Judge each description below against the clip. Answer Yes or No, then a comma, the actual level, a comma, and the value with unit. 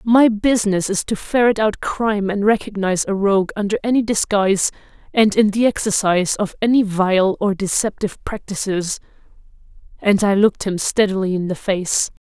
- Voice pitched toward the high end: Yes, high, 205 Hz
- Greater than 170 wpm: No, average, 155 wpm